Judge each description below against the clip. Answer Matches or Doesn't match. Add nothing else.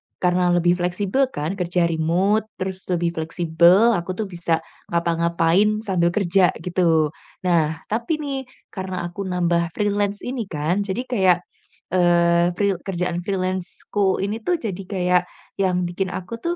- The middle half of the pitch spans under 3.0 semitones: Matches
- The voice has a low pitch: Doesn't match